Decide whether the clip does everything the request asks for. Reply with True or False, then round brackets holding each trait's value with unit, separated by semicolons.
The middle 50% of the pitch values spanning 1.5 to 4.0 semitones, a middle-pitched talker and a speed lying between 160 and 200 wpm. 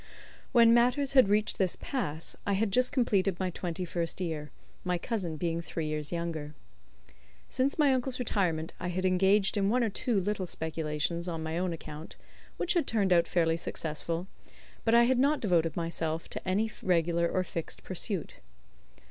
False (5.1 semitones; 180 Hz; 175 wpm)